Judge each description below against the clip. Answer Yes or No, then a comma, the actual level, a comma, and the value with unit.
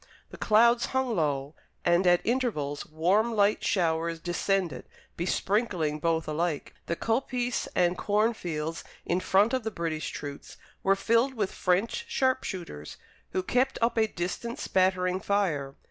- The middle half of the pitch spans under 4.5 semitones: No, wide, 5.5 semitones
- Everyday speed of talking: Yes, average, 145 wpm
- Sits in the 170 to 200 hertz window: Yes, medium, 185 Hz